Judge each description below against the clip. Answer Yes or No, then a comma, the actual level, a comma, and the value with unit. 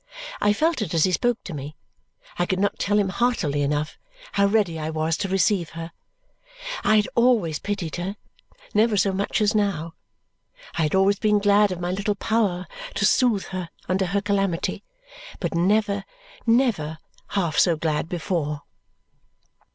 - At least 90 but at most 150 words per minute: No, average, 165 wpm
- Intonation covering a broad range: No, average, 3.9 semitones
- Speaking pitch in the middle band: No, high, 195 Hz